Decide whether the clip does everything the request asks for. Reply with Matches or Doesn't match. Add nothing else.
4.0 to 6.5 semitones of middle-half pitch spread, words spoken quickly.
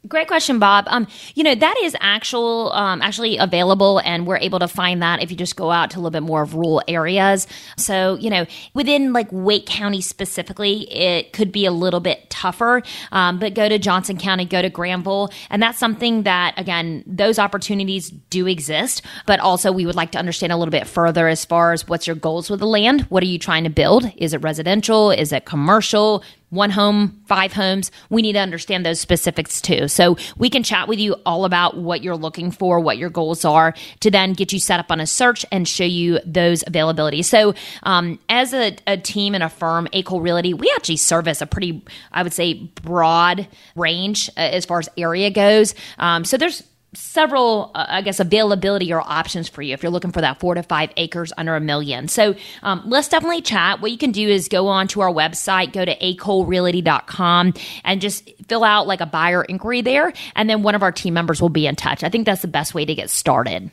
Doesn't match